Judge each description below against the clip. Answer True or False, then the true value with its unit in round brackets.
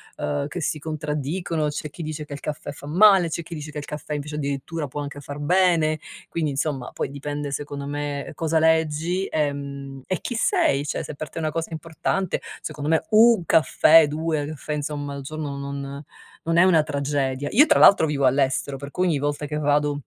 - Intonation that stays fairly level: True (2.2 semitones)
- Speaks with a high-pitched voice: False (150 Hz)